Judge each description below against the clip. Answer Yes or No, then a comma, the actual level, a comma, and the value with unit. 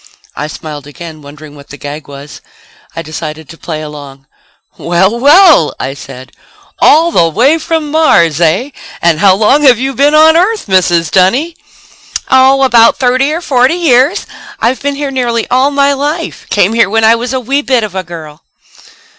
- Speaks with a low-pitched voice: No, high, 230 Hz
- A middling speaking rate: Yes, average, 180 wpm